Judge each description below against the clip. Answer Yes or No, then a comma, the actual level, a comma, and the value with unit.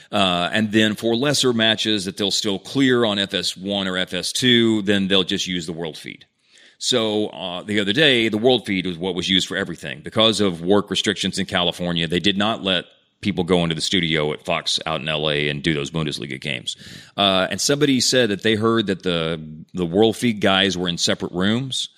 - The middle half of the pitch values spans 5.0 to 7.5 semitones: No, average, 3.6 semitones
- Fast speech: Yes, fast, 210 wpm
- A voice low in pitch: Yes, low, 100 Hz